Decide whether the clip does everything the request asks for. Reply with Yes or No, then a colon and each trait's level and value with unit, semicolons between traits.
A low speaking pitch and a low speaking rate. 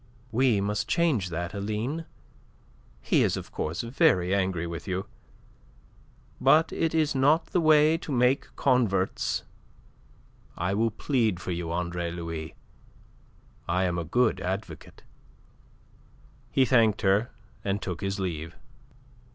Yes: low, 100 Hz; slow, 125 wpm